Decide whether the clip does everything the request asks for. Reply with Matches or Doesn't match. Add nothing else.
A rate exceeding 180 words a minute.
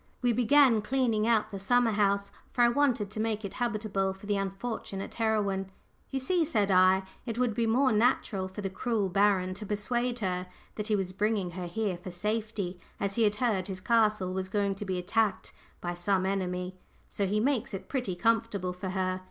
Matches